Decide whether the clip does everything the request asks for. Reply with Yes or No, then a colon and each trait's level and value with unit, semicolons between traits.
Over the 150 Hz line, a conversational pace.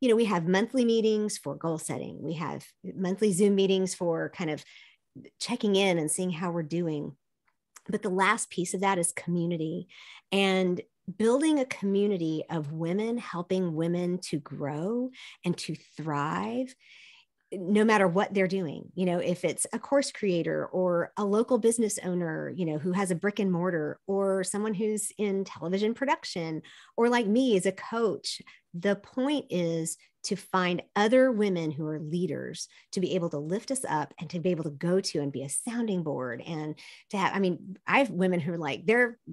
Yes: medium, 185 Hz; average, 190 wpm